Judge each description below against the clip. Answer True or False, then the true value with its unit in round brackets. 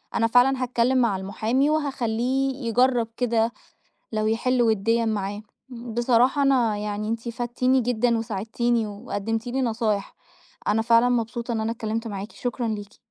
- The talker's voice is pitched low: False (230 Hz)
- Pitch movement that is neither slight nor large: False (2.1 semitones)